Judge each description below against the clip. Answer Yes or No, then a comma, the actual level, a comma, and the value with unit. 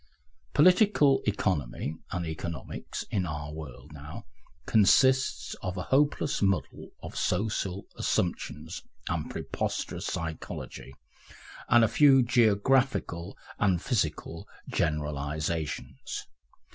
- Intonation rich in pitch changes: Yes, wide, 7.5 semitones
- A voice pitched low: Yes, very low, 95 Hz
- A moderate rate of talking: No, slow, 95 wpm